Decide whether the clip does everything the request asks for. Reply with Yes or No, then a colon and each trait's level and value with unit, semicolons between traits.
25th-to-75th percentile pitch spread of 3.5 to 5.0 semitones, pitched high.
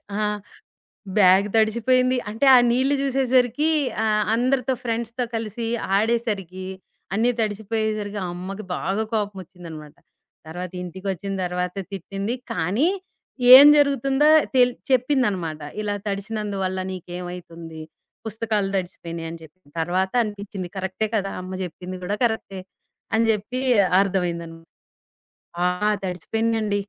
Yes: average, 3.9 semitones; high, 205 Hz